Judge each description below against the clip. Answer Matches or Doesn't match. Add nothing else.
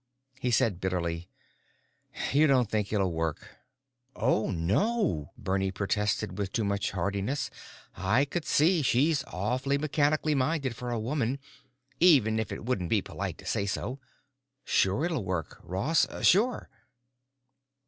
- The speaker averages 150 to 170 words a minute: Doesn't match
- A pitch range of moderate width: Doesn't match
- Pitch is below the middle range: Matches